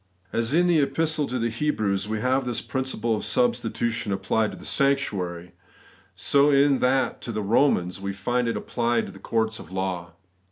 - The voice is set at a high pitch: No, low, 115 Hz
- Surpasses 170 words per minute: Yes, average, 185 wpm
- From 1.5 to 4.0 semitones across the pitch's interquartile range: No, average, 4.8 semitones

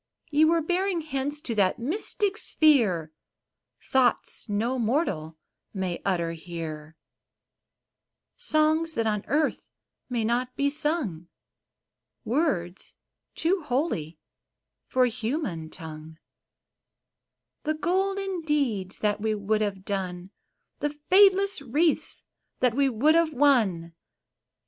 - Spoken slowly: Yes, slow, 115 wpm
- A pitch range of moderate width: No, wide, 8.6 semitones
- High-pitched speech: Yes, very high, 250 Hz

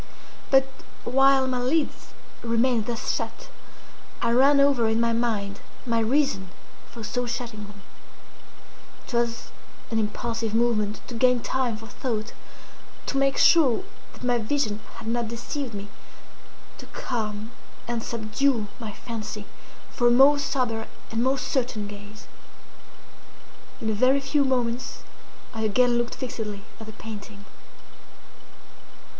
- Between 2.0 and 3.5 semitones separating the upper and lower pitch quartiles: Yes, average, 2.9 semitones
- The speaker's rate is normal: No, slow, 130 wpm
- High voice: Yes, high, 235 Hz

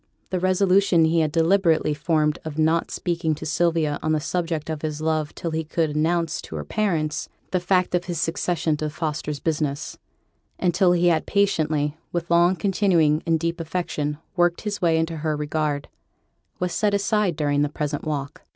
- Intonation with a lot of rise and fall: No, narrow, 2.5 semitones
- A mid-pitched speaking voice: Yes, medium, 160 Hz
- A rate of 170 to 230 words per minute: Yes, average, 180 wpm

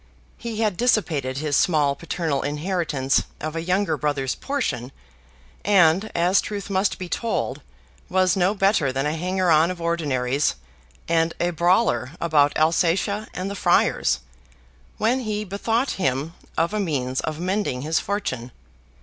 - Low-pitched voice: No, medium, 170 Hz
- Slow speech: No, average, 145 wpm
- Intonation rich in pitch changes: No, average, 5.0 semitones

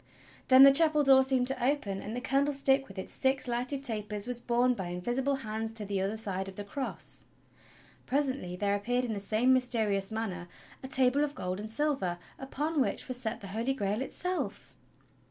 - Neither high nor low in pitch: No, high, 245 Hz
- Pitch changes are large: No, average, 4.6 semitones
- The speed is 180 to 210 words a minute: Yes, average, 190 wpm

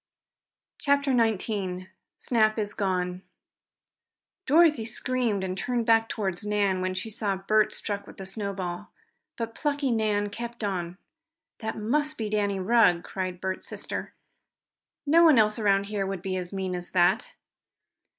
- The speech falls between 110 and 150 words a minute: Yes, average, 145 wpm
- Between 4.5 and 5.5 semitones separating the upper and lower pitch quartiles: No, average, 3.4 semitones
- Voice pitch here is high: Yes, high, 205 Hz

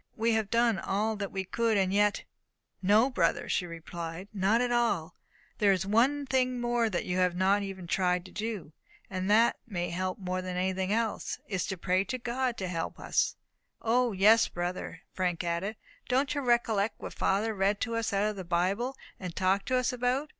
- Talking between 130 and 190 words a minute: No, fast, 205 wpm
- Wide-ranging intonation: No, average, 4.0 semitones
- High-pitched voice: Yes, high, 200 Hz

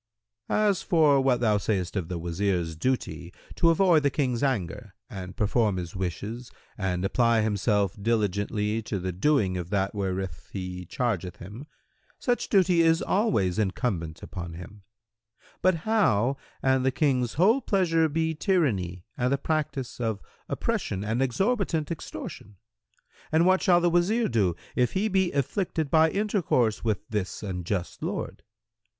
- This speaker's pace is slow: No, average, 150 wpm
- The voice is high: No, low, 115 Hz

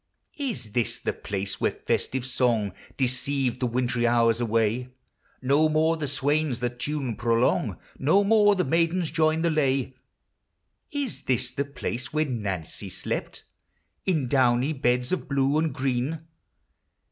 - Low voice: Yes, low, 130 Hz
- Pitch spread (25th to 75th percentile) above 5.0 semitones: No, average, 4.4 semitones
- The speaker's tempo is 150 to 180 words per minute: No, average, 140 wpm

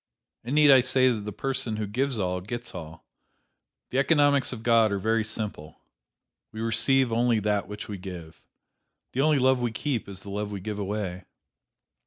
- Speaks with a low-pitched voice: Yes, low, 110 Hz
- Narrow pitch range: No, average, 4.3 semitones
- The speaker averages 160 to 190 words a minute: Yes, average, 185 wpm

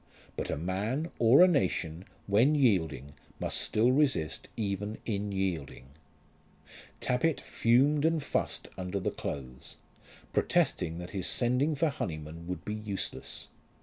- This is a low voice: Yes, low, 105 Hz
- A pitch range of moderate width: No, wide, 7.2 semitones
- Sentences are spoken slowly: Yes, slow, 130 wpm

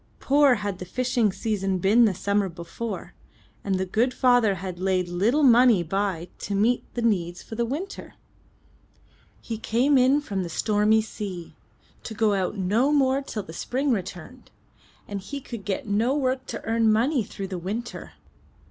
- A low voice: No, high, 215 Hz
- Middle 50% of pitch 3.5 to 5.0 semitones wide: Yes, average, 4.5 semitones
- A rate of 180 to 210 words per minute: No, average, 170 wpm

